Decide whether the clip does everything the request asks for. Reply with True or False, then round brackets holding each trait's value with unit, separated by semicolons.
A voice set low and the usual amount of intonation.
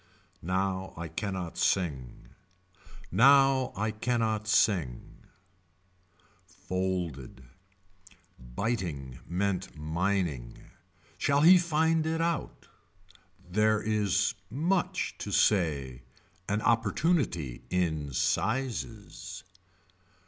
False (100 Hz; 6.7 semitones)